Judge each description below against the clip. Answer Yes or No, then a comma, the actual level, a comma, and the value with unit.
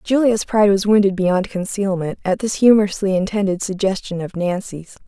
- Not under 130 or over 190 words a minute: Yes, average, 155 wpm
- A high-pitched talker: Yes, high, 195 Hz